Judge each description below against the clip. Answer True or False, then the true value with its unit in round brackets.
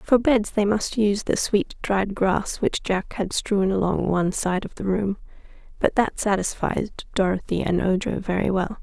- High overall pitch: True (200 Hz)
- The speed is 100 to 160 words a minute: False (185 wpm)